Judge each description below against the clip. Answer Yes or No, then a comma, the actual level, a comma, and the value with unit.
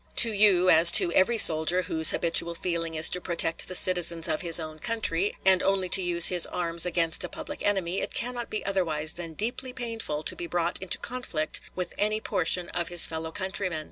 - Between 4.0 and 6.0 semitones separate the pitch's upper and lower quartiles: No, average, 2.8 semitones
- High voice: No, medium, 175 Hz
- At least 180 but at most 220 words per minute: Yes, fast, 205 wpm